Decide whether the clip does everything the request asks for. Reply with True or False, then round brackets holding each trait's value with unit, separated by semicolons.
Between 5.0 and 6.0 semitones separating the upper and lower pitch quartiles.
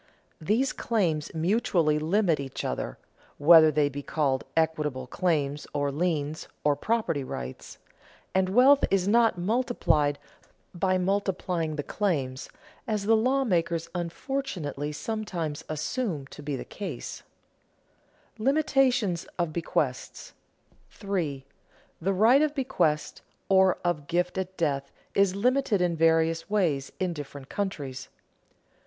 True (5.5 semitones)